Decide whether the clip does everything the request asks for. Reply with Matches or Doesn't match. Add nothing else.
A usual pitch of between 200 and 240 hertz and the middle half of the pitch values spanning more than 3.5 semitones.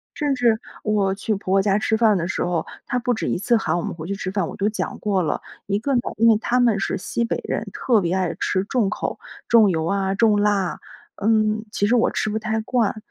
Doesn't match